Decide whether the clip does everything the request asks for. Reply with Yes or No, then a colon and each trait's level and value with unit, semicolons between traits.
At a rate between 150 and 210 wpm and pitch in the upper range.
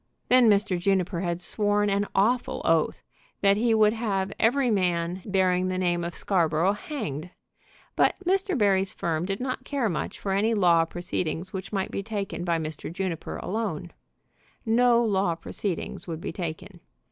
Yes: average, 160 wpm; high, 195 Hz